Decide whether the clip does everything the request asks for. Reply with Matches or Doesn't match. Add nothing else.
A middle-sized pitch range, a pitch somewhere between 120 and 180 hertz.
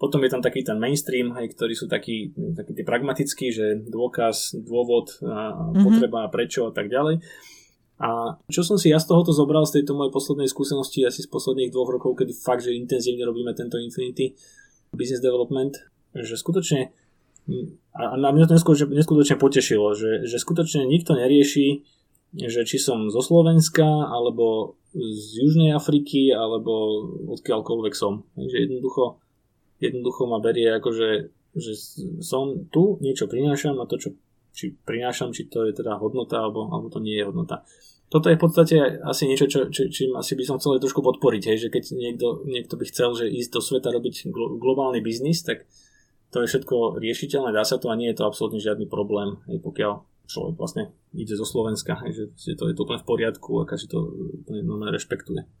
Matches